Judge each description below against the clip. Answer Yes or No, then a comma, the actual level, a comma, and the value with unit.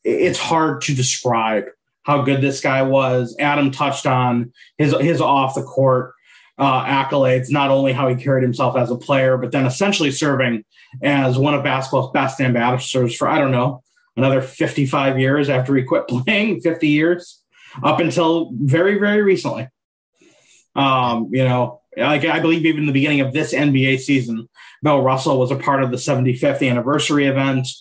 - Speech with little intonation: Yes, narrow, 2.2 semitones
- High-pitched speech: No, low, 135 Hz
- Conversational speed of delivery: Yes, average, 175 wpm